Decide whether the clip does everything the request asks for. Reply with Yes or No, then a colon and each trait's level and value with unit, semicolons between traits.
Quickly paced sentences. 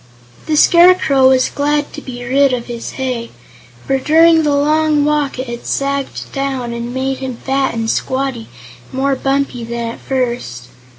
No: average, 170 wpm